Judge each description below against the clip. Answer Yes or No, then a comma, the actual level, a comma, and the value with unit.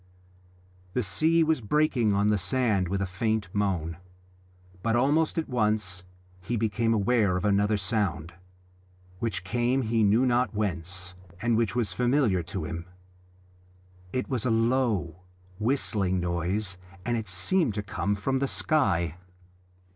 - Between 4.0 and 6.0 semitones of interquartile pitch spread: Yes, average, 4.5 semitones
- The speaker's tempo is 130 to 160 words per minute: Yes, average, 140 wpm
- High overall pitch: No, low, 105 Hz